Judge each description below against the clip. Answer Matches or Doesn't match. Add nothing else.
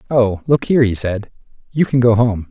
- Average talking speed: Doesn't match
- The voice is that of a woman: Doesn't match